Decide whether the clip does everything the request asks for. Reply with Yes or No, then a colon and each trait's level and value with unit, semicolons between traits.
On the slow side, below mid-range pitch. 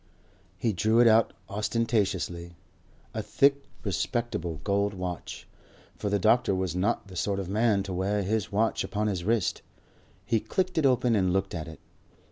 No: average, 165 wpm; low, 100 Hz